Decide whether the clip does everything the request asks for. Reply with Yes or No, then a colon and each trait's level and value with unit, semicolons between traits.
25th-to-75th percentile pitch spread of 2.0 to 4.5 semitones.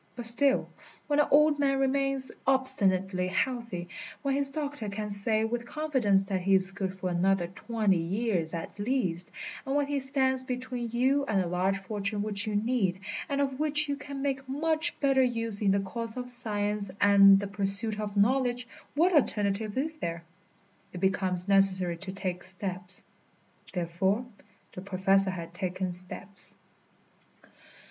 No: wide, 5.6 semitones